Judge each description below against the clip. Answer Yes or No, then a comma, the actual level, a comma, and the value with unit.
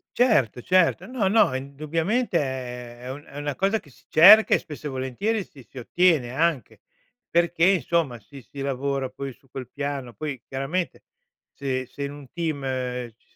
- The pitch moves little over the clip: No, average, 4.6 semitones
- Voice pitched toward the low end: No, medium, 145 Hz